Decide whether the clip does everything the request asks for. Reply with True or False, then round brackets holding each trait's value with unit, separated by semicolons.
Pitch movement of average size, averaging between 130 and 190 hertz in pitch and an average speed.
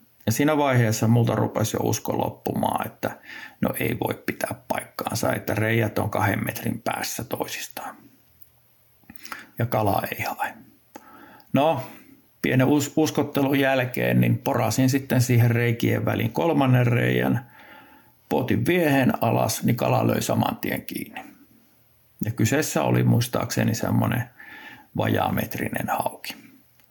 False (3.7 semitones; 115 Hz; 120 wpm)